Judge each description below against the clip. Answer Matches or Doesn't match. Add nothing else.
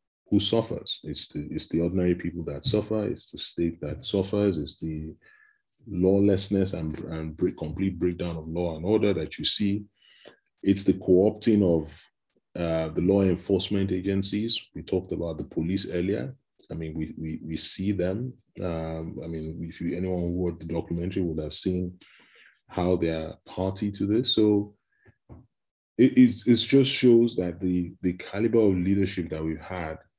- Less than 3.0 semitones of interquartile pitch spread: Doesn't match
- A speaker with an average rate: Matches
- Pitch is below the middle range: Matches